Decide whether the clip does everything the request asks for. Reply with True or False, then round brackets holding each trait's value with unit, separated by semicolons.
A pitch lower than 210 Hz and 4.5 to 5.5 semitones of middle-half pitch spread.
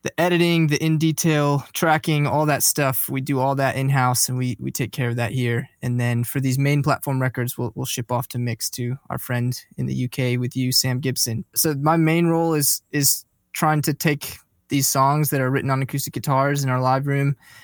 False (135 Hz; 2.7 semitones)